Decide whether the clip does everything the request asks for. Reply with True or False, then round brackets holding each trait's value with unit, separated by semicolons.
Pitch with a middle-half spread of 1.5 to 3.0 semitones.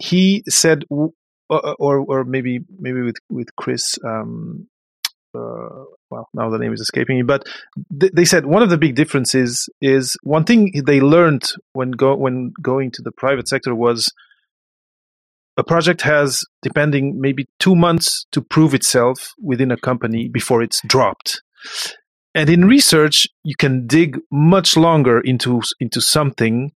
False (4.6 semitones)